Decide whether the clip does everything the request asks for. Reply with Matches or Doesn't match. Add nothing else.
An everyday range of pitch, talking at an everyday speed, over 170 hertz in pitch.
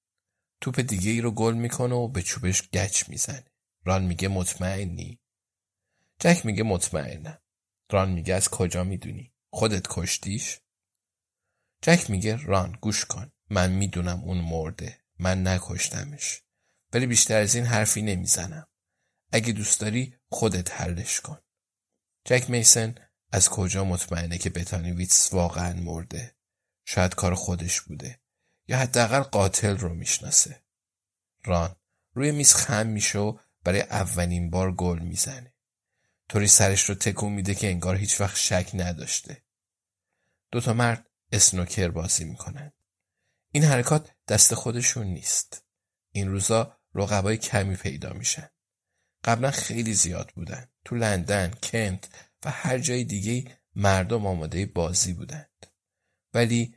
Doesn't match